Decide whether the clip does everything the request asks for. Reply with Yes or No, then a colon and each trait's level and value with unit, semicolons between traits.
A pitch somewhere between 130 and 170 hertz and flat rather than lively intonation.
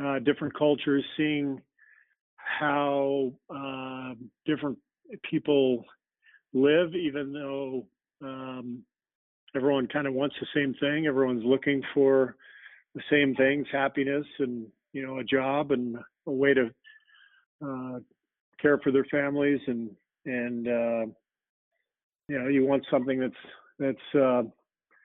Yes: low, 135 Hz; narrow, 1.9 semitones